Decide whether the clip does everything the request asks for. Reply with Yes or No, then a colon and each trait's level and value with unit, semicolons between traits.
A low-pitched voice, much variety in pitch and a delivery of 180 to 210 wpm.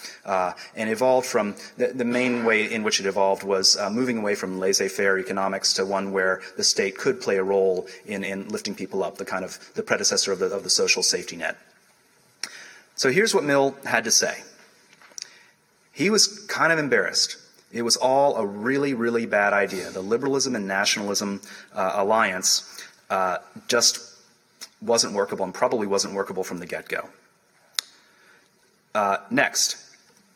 No: low, 105 Hz; wide, 5.9 semitones; average, 165 wpm